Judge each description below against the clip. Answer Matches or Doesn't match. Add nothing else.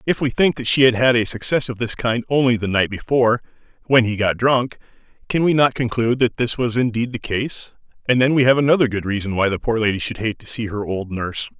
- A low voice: Matches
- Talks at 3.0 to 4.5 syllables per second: Doesn't match